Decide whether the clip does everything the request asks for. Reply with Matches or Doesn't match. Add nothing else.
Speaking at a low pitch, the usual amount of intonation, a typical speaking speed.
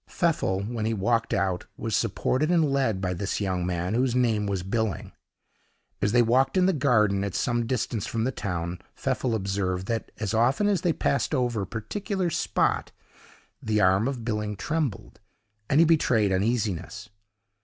Matches